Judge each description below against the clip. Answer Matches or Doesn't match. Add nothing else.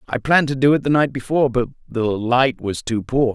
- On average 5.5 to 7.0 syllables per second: Matches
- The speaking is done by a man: Matches